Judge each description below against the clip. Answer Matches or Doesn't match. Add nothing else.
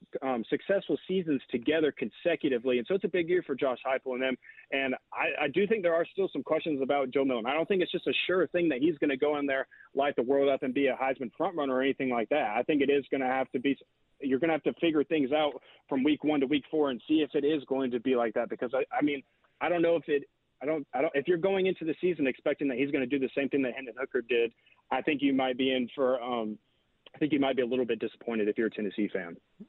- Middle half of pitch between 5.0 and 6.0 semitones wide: Doesn't match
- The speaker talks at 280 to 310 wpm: Matches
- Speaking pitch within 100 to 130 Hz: Doesn't match